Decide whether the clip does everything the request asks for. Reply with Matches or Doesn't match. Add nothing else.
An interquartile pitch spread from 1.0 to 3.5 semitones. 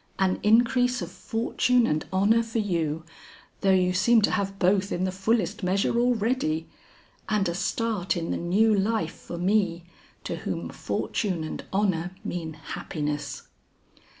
Doesn't match